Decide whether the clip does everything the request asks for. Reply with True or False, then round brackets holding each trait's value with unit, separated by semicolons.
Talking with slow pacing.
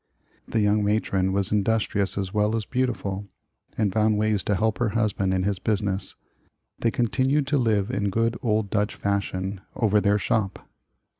False (165 wpm)